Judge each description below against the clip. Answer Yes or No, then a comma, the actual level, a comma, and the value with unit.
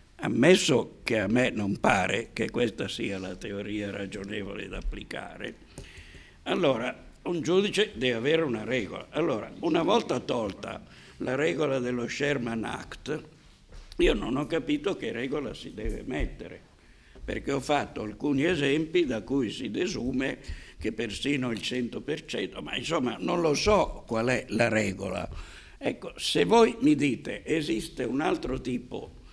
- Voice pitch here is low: Yes, low, 125 Hz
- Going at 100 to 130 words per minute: No, average, 145 wpm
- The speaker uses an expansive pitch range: Yes, wide, 6.3 semitones